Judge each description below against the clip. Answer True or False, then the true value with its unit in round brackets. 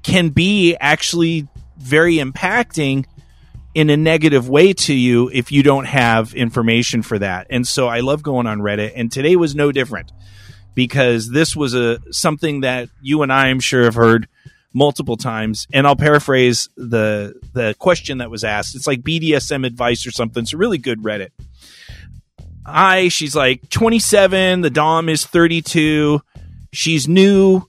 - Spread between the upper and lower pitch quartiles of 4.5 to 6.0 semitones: True (5.1 semitones)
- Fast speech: False (165 wpm)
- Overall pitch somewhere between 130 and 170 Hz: True (135 Hz)